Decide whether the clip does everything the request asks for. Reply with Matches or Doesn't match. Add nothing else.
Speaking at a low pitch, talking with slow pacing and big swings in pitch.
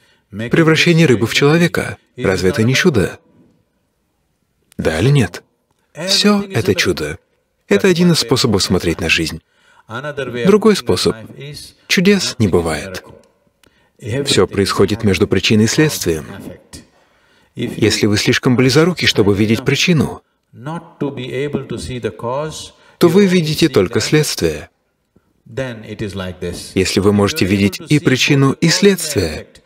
Matches